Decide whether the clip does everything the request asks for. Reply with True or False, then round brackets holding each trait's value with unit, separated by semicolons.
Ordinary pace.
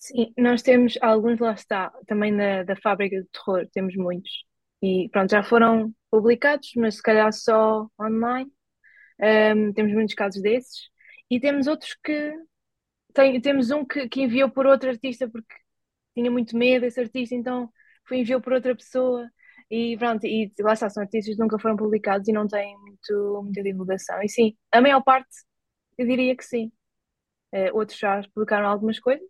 True (175 wpm)